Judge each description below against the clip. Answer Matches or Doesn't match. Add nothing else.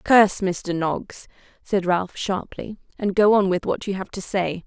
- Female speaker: Matches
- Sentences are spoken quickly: Doesn't match